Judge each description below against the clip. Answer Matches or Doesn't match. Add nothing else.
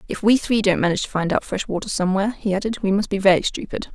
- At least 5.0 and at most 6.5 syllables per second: Doesn't match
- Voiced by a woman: Matches